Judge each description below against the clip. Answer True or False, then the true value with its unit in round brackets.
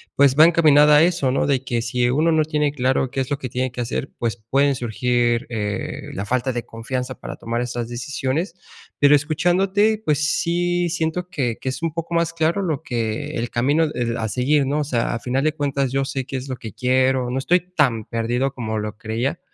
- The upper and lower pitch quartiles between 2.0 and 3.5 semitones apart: False (4.2 semitones)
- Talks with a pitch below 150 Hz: True (135 Hz)